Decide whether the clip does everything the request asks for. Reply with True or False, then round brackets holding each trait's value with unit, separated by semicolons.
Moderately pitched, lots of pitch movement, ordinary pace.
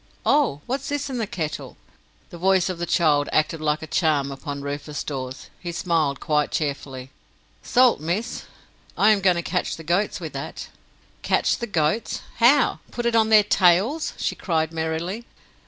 True (170 Hz; 6.1 semitones; 170 wpm)